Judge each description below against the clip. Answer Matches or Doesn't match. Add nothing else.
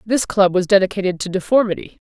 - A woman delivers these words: Matches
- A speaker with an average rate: Matches